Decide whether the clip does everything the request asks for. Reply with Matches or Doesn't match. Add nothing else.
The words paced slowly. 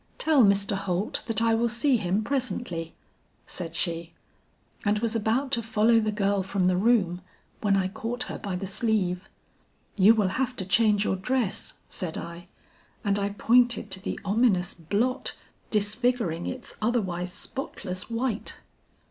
Doesn't match